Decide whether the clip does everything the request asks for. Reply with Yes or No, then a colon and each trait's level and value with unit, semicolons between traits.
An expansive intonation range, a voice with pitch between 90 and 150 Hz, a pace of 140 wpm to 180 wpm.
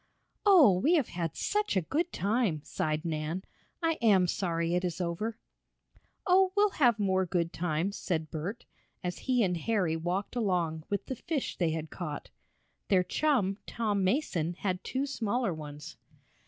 No: wide, 6.0 semitones; high, 190 Hz; average, 160 wpm